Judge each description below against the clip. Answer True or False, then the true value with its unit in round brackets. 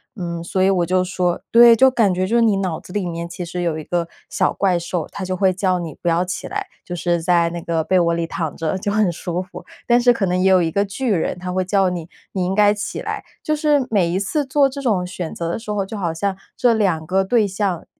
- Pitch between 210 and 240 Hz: False (185 Hz)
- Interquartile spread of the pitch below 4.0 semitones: True (3.1 semitones)